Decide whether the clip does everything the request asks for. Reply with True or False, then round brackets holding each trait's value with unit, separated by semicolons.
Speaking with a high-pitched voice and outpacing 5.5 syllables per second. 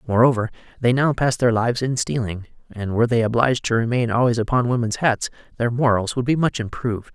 False (120 Hz; 6.1 syllables/s)